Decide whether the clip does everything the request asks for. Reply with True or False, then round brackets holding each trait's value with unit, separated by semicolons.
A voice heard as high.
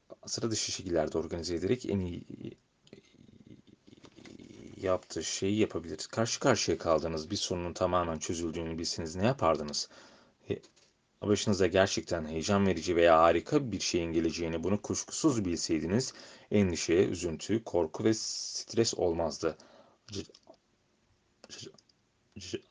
False (90 Hz)